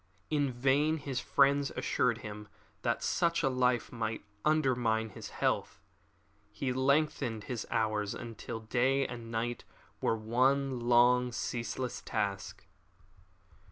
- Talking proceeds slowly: Yes, slow, 120 wpm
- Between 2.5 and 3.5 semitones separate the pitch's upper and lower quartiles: Yes, average, 3.2 semitones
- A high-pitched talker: No, low, 125 Hz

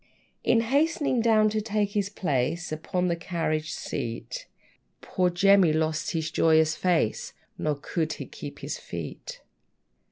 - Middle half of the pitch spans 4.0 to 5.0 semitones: Yes, average, 4.6 semitones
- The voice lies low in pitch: No, medium, 175 Hz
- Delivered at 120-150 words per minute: Yes, slow, 135 wpm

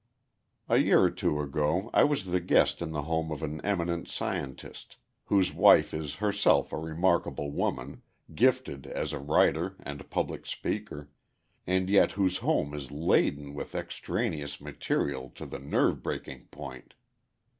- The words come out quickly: No, average, 150 wpm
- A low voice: Yes, very low, 80 Hz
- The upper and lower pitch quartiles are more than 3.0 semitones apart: Yes, average, 4.3 semitones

